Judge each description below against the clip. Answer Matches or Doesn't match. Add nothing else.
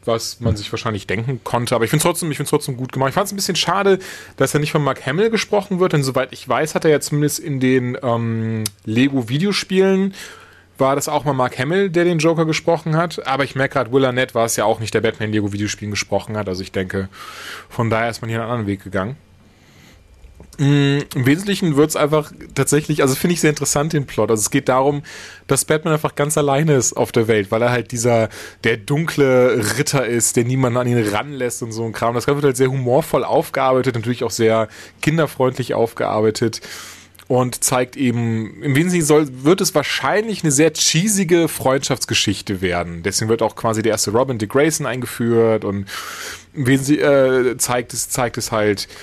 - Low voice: Matches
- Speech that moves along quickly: Matches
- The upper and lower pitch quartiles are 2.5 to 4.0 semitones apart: Doesn't match